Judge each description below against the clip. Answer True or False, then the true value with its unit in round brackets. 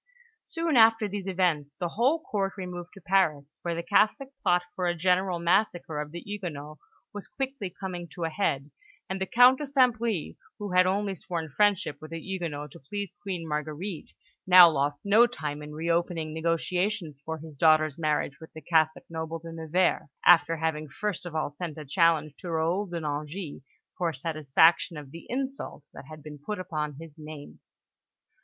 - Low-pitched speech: False (170 Hz)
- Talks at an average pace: True (180 wpm)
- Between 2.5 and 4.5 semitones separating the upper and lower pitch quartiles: True (3.9 semitones)